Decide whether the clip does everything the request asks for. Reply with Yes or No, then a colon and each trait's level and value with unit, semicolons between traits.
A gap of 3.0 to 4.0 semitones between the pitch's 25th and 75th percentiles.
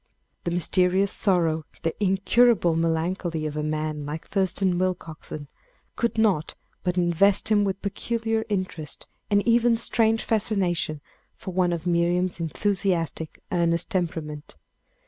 Yes: average, 3.6 semitones